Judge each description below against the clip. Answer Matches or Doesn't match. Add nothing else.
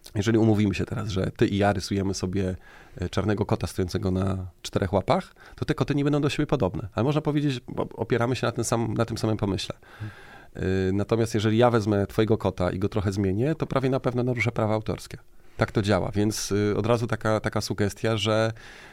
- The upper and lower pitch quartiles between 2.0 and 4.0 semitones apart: Matches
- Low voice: Matches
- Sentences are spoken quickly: Matches